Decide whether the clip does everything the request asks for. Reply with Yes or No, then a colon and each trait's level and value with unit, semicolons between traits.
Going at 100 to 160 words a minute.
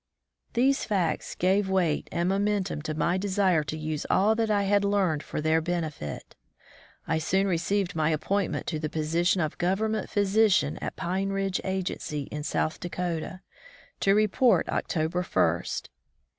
Yes: average, 150 wpm